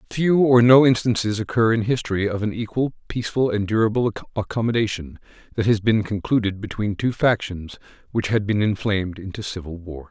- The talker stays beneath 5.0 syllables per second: No, 5.7 syllables/s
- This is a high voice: No, low, 105 Hz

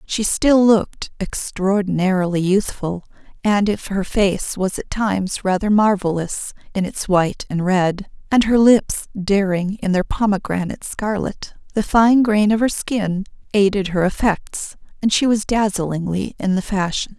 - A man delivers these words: No, female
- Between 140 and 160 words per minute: Yes, average, 150 wpm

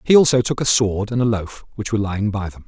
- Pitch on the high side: No, low, 110 Hz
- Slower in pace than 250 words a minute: No, fast, 290 wpm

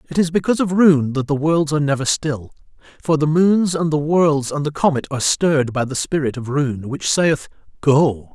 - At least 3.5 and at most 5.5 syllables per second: Yes, 5.2 syllables/s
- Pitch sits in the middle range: Yes, medium, 150 Hz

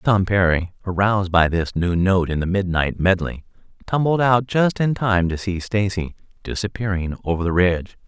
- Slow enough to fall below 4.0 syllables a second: No, 5.0 syllables/s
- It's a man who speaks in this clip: Yes, male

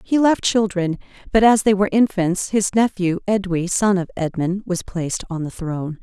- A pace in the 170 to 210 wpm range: Yes, average, 190 wpm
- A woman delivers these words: Yes, female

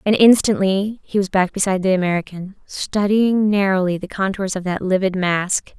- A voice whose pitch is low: No, high, 195 Hz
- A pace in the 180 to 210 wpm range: No, average, 165 wpm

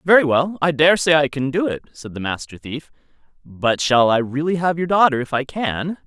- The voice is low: No, medium, 150 Hz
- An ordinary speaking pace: No, fast, 220 wpm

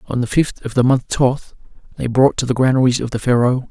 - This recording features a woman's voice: No, male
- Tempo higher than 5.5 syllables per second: Yes, 5.7 syllables/s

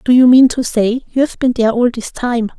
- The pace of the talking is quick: Yes, fast, 255 wpm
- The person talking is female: Yes, female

